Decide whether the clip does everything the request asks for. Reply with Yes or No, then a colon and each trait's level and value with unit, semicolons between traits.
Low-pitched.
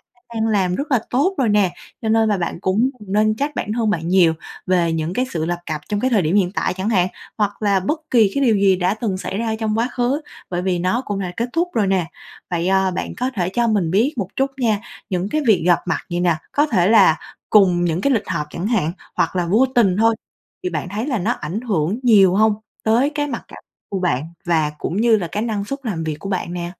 No: high, 200 Hz